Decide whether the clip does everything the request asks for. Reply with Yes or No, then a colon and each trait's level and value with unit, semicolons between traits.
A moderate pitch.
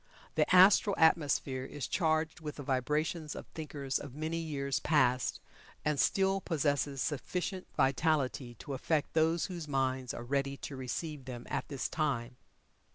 Yes: medium, 145 Hz